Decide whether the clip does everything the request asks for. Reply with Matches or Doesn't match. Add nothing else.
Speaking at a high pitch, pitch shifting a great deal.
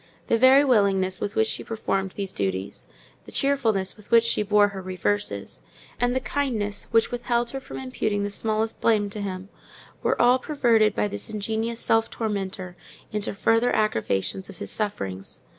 Doesn't match